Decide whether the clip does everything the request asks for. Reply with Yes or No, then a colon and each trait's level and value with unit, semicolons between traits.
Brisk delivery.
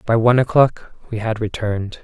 No: average, 175 wpm